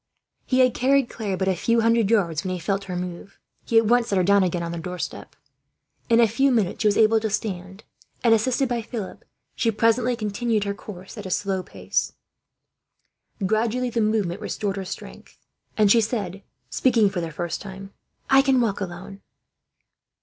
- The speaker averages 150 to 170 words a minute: No, average, 190 wpm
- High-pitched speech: Yes, high, 210 Hz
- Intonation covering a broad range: No, average, 3.4 semitones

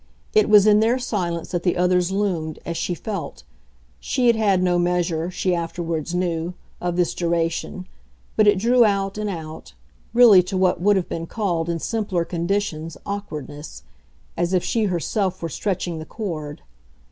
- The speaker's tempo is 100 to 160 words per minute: No, average, 170 wpm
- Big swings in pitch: No, average, 3.4 semitones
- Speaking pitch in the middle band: Yes, medium, 180 Hz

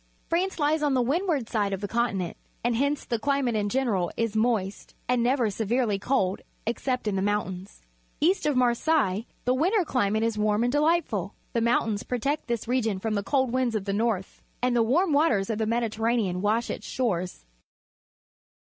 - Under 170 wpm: No, average, 190 wpm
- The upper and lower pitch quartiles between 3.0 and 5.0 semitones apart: Yes, average, 4.2 semitones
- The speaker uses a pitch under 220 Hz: No, high, 235 Hz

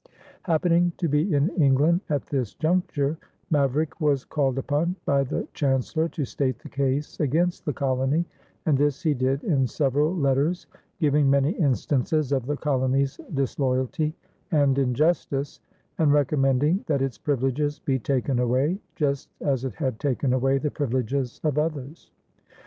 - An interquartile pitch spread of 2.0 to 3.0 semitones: Yes, narrow, 2.4 semitones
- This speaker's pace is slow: No, average, 150 wpm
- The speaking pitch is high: No, medium, 140 Hz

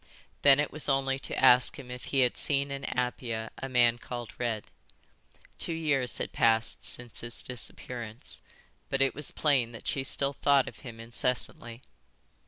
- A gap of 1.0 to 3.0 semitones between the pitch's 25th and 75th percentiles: Yes, narrow, 2.5 semitones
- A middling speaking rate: Yes, average, 170 wpm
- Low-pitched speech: Yes, low, 125 Hz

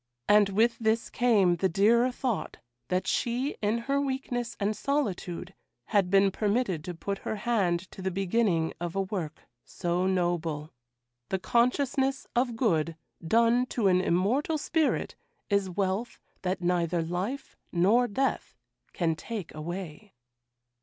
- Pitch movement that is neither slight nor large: Yes, average, 4.9 semitones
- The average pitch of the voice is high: Yes, high, 200 Hz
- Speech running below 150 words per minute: Yes, average, 140 wpm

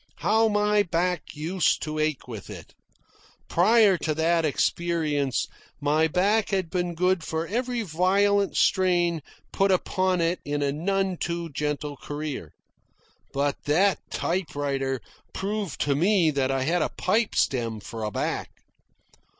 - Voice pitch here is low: No, medium, 170 Hz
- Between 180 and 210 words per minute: No, average, 140 wpm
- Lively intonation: No, average, 4.5 semitones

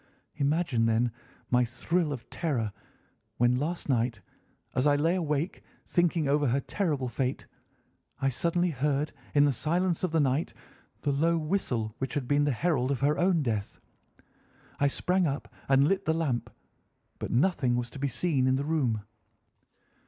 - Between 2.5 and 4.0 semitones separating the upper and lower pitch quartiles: No, average, 4.5 semitones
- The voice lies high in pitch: No, medium, 145 Hz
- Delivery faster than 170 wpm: No, average, 165 wpm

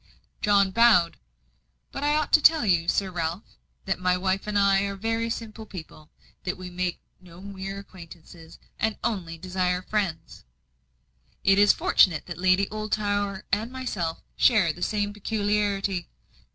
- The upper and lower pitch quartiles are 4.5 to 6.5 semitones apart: No, average, 2.7 semitones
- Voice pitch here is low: No, high, 195 Hz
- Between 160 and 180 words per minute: No, average, 150 wpm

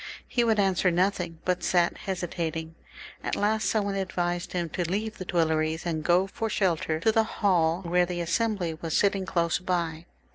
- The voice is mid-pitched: Yes, medium, 180 Hz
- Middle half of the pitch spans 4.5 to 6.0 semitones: No, average, 2.7 semitones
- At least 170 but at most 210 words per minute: Yes, average, 180 wpm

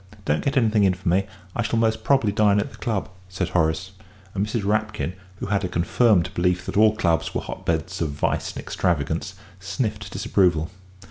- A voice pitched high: No, very low, 95 Hz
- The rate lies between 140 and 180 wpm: No, average, 190 wpm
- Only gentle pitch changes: No, average, 3.6 semitones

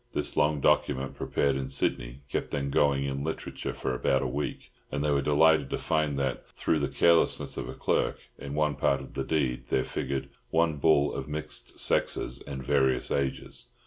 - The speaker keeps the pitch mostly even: Yes, narrow, 1.8 semitones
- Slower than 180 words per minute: No, average, 190 wpm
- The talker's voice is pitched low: Yes, very low, 70 Hz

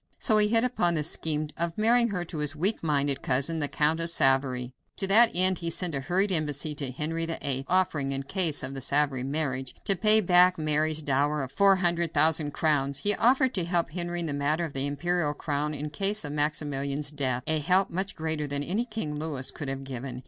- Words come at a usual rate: No, fast, 220 wpm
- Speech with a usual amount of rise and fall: Yes, average, 3.9 semitones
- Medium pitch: Yes, medium, 155 Hz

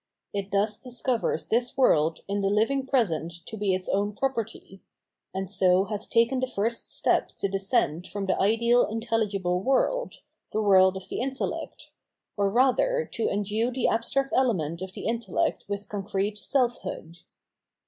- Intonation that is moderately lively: Yes, average, 4.0 semitones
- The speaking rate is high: No, average, 160 wpm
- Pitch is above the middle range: Yes, high, 210 Hz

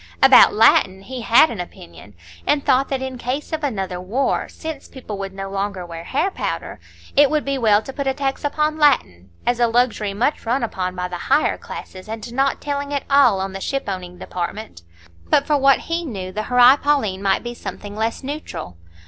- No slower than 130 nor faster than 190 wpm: No, fast, 205 wpm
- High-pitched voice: Yes, high, 240 Hz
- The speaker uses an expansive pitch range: Yes, wide, 6.2 semitones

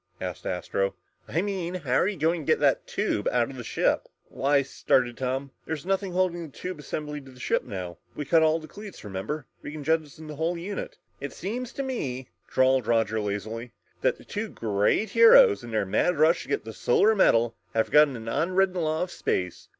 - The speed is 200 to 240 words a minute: Yes, fast, 205 wpm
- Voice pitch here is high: No, medium, 150 Hz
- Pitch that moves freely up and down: Yes, wide, 6.9 semitones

